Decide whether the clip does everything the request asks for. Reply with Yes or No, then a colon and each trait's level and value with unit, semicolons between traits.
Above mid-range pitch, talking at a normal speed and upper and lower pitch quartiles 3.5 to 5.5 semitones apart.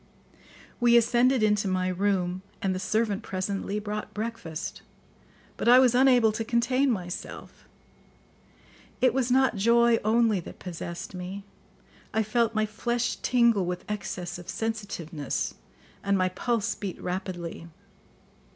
No: high, 210 Hz; slow, 130 wpm; average, 4.2 semitones